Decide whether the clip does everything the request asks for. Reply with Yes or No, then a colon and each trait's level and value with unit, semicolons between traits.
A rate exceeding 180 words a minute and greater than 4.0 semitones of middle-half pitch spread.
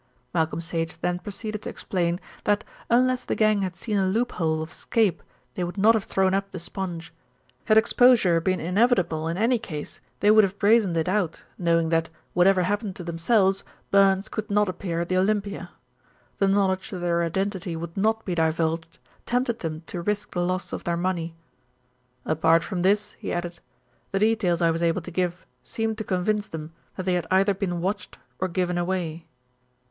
No: average, 190 wpm; average, 3.3 semitones